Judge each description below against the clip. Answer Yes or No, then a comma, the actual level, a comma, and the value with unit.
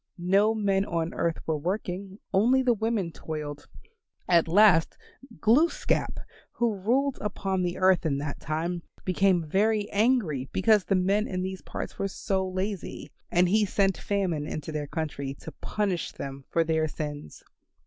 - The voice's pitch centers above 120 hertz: Yes, medium, 185 Hz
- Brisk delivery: No, average, 155 wpm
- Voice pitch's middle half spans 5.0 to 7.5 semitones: No, average, 4.2 semitones